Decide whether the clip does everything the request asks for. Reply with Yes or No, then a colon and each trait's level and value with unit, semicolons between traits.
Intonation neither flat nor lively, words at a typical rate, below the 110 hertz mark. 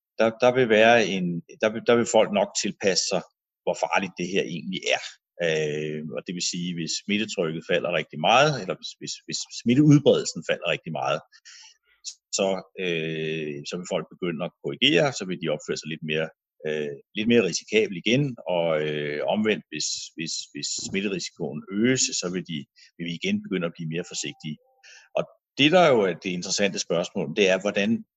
No: wide, 6.8 semitones; average, 180 wpm; very low, 95 Hz